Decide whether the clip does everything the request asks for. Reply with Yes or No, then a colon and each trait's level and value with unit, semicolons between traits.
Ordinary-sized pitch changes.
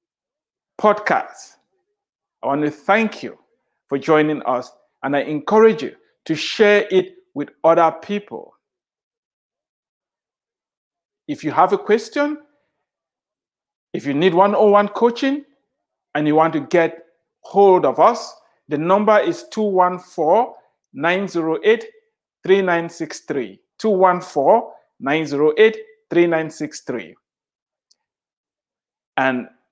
No: wide, 6.2 semitones